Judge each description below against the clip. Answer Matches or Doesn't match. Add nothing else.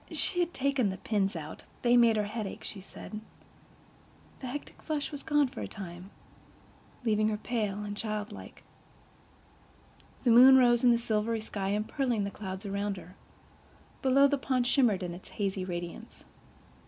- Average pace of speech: Matches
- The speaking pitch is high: Matches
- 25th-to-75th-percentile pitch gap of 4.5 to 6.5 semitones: Doesn't match